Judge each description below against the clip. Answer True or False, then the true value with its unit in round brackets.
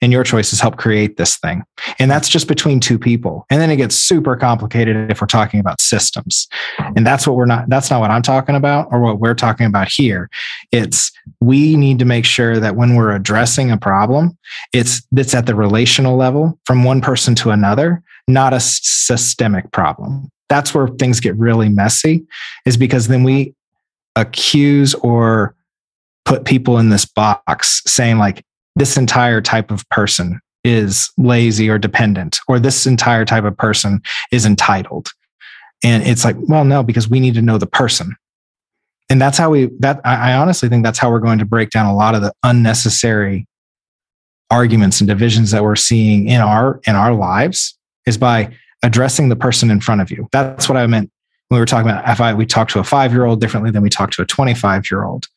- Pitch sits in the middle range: False (120 Hz)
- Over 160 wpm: True (195 wpm)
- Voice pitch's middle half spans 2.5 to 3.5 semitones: True (3.2 semitones)